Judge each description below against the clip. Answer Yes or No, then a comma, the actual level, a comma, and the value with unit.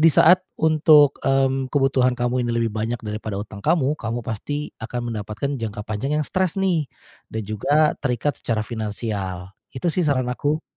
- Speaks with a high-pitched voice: No, low, 125 Hz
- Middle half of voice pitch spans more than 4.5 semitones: Yes, average, 5.2 semitones